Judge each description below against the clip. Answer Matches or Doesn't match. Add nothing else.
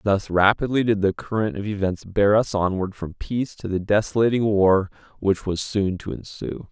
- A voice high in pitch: Doesn't match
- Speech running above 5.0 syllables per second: Doesn't match